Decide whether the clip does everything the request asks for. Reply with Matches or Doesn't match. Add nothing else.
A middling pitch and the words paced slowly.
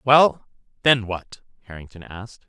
Doesn't match